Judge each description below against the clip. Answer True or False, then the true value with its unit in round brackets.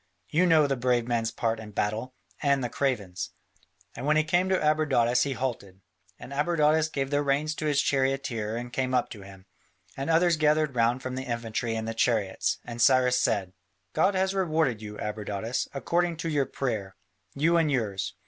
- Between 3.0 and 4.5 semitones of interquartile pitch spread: False (5.0 semitones)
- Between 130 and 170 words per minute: False (185 wpm)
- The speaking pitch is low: True (130 Hz)